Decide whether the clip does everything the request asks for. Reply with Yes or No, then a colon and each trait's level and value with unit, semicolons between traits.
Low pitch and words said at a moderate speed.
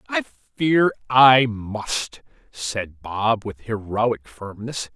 No: low, 110 Hz; slow, 110 wpm